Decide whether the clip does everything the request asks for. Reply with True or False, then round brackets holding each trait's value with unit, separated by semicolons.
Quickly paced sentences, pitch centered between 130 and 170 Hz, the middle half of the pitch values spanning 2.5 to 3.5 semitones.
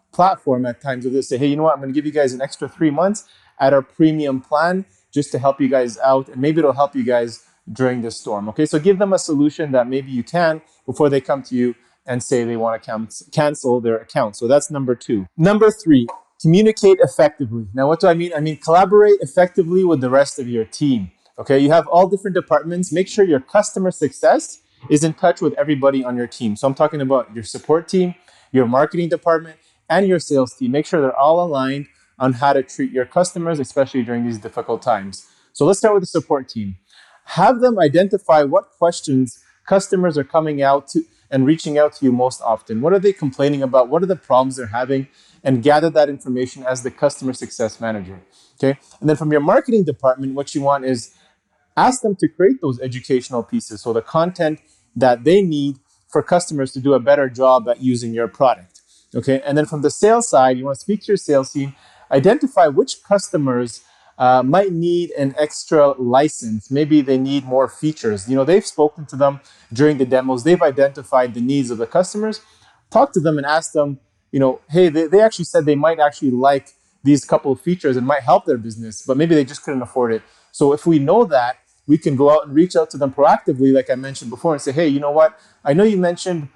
False (220 wpm; 140 Hz; 4.2 semitones)